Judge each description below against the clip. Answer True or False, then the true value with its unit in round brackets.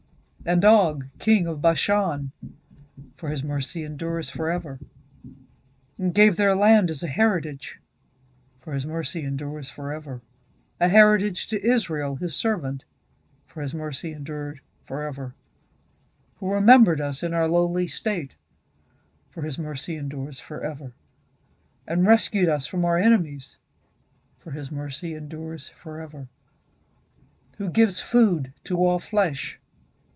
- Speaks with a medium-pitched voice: True (155 Hz)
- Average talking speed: False (125 wpm)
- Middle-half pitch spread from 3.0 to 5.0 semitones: True (4.2 semitones)